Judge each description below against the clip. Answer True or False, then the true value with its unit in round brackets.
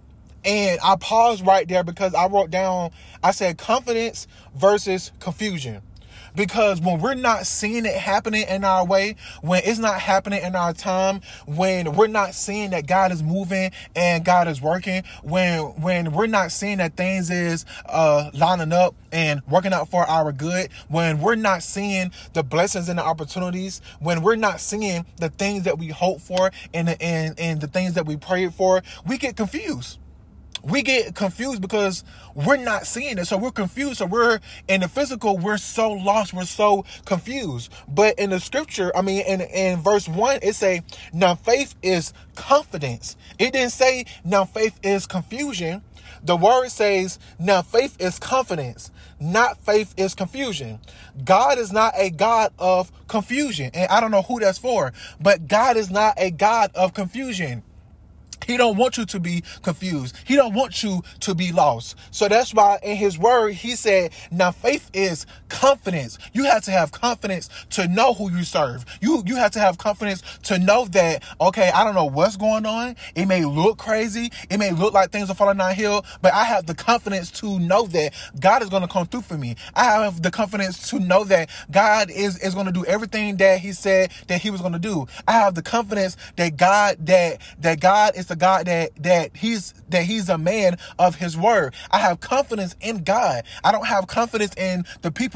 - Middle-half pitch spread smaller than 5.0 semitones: True (3.3 semitones)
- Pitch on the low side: False (190 Hz)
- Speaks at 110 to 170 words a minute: False (195 wpm)